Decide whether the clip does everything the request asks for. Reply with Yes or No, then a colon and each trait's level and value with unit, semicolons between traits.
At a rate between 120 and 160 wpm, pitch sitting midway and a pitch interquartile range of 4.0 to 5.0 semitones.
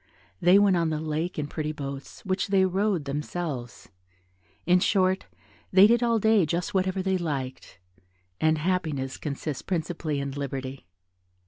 Yes: average, 145 wpm; medium, 165 Hz; average, 4.7 semitones